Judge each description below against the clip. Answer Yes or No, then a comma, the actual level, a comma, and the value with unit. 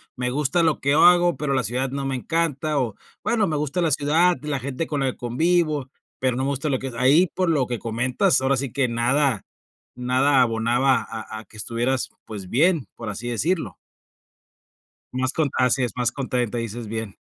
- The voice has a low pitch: Yes, low, 130 Hz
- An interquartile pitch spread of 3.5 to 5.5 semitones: Yes, average, 3.8 semitones